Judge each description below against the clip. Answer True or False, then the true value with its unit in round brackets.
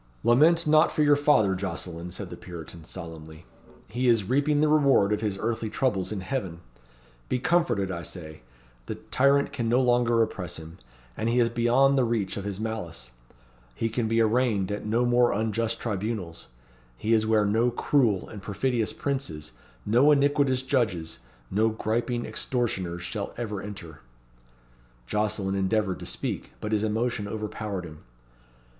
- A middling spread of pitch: True (4.3 semitones)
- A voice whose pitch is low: True (110 Hz)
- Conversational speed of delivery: True (155 wpm)